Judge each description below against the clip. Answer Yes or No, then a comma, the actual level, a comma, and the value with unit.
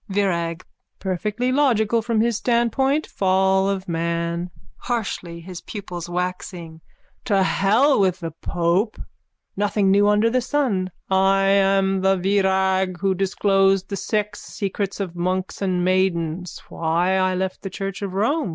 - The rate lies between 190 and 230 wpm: No, average, 140 wpm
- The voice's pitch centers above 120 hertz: Yes, high, 190 Hz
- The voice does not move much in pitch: Yes, narrow, 2.2 semitones